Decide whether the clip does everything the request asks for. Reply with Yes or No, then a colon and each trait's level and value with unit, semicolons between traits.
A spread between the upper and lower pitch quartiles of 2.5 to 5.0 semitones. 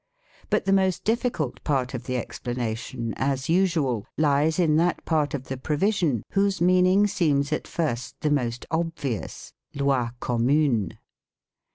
No: wide, 5.4 semitones